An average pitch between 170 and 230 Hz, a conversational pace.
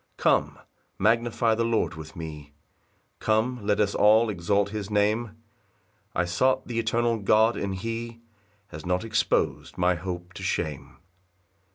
No: low, 105 Hz; average, 145 wpm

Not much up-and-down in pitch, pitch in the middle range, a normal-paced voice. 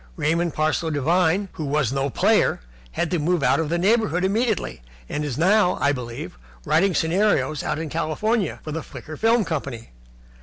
No: average, 4.2 semitones; medium, 160 Hz; average, 175 wpm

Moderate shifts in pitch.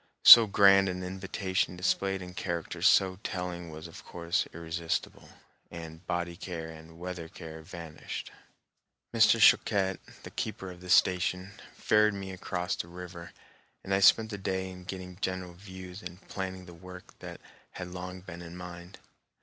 No: narrow, 1.5 semitones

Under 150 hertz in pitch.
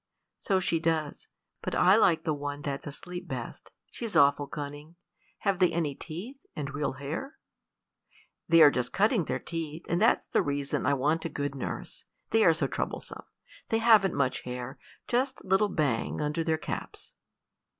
No: medium, 160 Hz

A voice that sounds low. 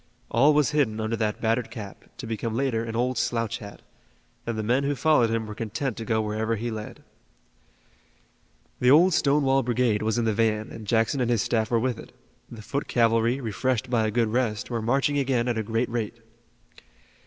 Yes: low, 115 Hz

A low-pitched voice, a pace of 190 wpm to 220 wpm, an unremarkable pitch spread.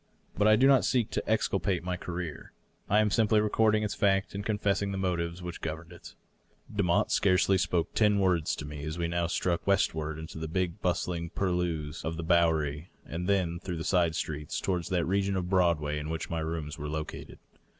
Yes: very low, 90 Hz; average, 200 wpm; average, 3.3 semitones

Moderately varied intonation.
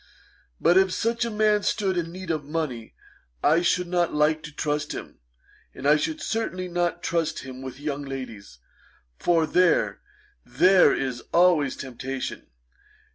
Yes: average, 4.5 semitones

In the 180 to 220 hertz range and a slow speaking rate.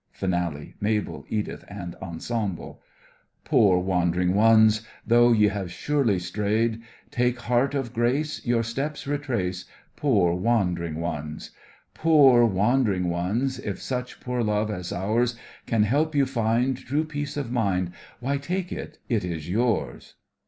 No: low, 110 Hz; slow, 130 wpm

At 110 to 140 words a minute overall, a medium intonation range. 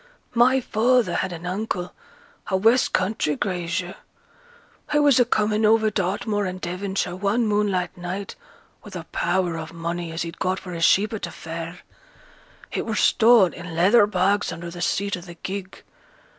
No: average, 170 wpm; average, 3.3 semitones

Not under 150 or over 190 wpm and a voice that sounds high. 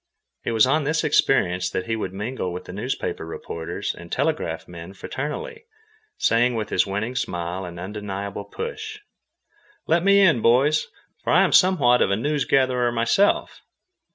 No: average, 160 wpm; low, 115 Hz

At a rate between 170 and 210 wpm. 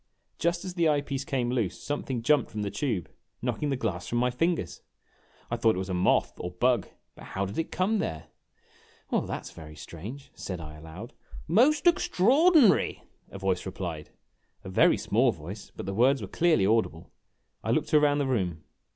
Yes: average, 190 wpm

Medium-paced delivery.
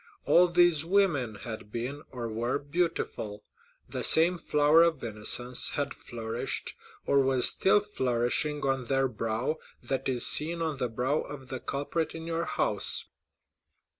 Yes: average, 145 wpm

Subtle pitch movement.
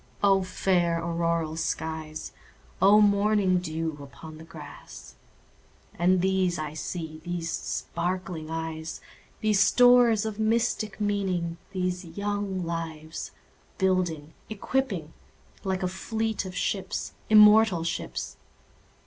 No: average, 3.8 semitones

